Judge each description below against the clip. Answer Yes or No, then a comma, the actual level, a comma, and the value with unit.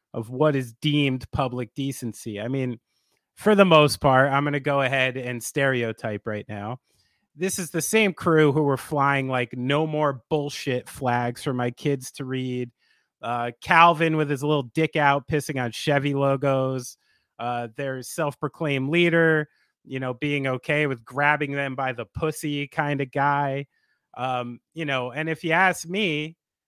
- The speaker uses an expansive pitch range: No, average, 3.2 semitones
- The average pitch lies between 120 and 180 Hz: Yes, medium, 140 Hz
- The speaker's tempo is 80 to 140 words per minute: No, average, 170 wpm